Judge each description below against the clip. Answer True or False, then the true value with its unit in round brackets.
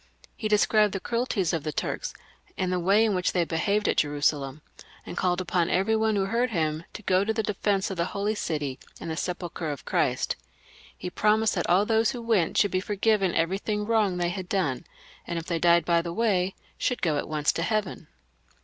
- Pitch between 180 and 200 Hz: True (185 Hz)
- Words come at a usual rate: False (215 wpm)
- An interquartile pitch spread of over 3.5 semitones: True (3.9 semitones)